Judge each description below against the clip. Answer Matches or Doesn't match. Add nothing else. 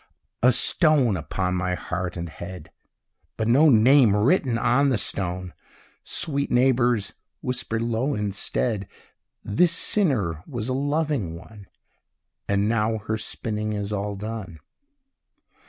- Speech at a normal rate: Doesn't match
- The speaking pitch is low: Matches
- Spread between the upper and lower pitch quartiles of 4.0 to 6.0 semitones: Matches